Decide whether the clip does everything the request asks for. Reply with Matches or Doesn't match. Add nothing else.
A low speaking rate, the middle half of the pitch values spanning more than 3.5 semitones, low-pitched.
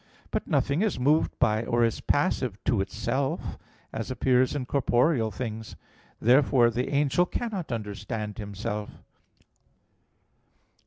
Matches